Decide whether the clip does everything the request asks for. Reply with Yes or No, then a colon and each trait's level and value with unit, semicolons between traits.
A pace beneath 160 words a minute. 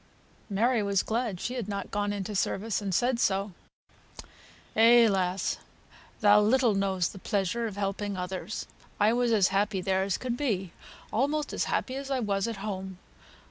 No: average, 170 wpm